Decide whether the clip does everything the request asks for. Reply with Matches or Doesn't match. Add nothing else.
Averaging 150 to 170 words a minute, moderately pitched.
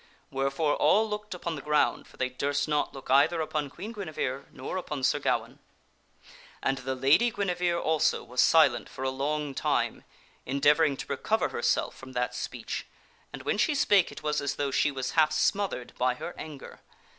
Doesn't match